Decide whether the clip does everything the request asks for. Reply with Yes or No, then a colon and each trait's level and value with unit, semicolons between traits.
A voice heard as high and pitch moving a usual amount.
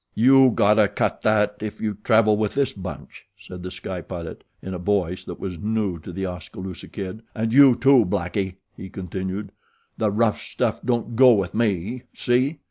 No: low, 105 Hz; average, 3.6 semitones